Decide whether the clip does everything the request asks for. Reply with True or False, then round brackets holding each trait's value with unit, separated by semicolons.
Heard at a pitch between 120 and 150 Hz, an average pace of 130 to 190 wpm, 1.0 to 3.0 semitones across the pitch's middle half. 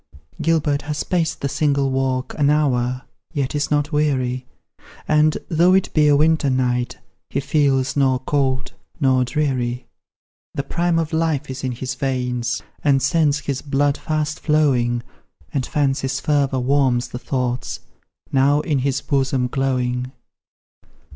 True (140 Hz; 140 wpm; 2.6 semitones)